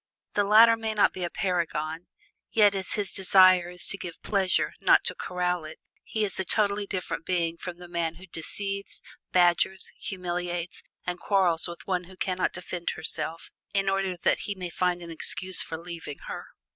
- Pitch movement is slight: Yes, narrow, 2.1 semitones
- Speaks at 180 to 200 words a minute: Yes, average, 185 wpm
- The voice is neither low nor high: Yes, medium, 180 Hz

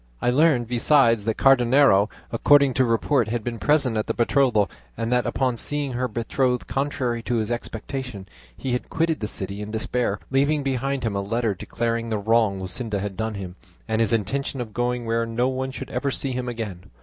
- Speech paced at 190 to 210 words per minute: Yes, average, 195 wpm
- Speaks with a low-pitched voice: Yes, low, 120 Hz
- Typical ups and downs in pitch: Yes, average, 3.1 semitones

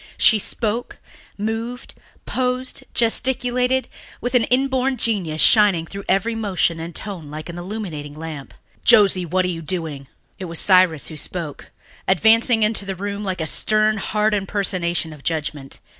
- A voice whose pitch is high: Yes, high, 195 Hz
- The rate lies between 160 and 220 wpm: No, average, 150 wpm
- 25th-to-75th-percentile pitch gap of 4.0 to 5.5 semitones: Yes, average, 5.2 semitones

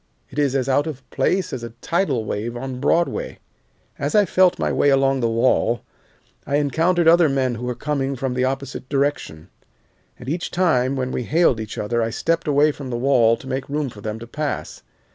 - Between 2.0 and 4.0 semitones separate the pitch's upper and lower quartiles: Yes, average, 3.7 semitones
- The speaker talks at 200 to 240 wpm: Yes, fast, 205 wpm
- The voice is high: No, low, 135 Hz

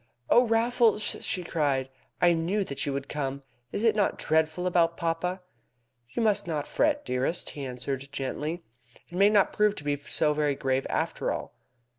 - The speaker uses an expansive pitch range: Yes, wide, 6.1 semitones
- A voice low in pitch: No, medium, 165 Hz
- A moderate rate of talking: Yes, average, 175 wpm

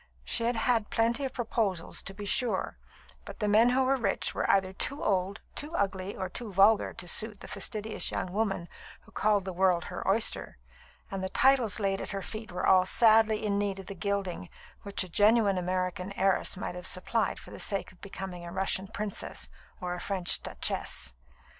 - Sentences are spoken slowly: No, average, 195 wpm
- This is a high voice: Yes, high, 200 Hz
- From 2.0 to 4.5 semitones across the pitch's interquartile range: Yes, average, 2.9 semitones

